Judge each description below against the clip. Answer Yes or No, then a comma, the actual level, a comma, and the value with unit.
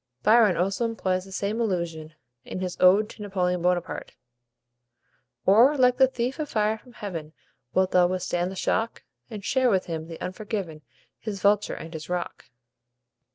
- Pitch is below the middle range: No, high, 190 Hz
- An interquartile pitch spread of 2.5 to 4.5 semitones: Yes, average, 3.6 semitones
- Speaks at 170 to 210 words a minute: No, average, 160 wpm